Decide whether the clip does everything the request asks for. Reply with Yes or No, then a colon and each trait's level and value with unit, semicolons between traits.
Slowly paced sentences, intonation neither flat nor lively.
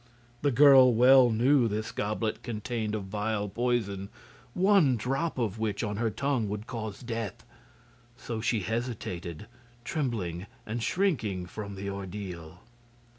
Yes: slow, 130 wpm; average, 3.5 semitones